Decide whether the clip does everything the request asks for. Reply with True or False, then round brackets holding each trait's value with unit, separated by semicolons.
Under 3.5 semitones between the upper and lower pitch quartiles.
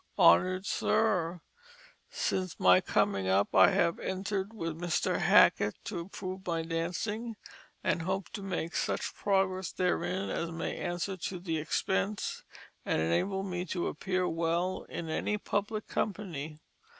True (2.8 semitones)